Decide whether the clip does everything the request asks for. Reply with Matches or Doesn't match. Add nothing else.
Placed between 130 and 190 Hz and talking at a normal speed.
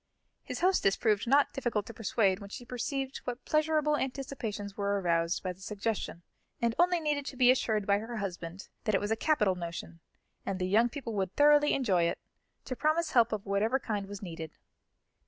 Doesn't match